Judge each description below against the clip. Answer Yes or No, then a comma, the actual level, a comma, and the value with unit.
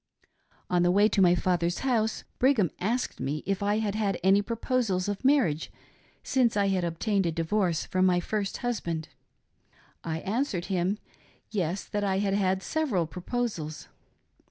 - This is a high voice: Yes, high, 195 Hz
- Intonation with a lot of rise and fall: No, average, 3.6 semitones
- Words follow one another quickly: No, average, 165 wpm